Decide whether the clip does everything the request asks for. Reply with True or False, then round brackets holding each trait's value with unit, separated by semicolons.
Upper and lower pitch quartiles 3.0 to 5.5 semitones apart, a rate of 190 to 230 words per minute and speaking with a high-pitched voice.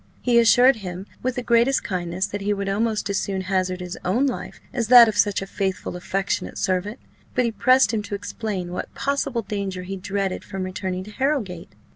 True (3.8 semitones; 200 wpm; 200 Hz)